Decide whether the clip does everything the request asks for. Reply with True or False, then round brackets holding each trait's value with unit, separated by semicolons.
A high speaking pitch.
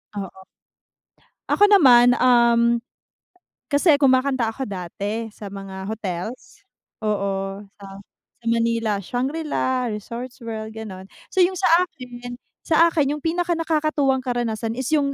True (240 Hz)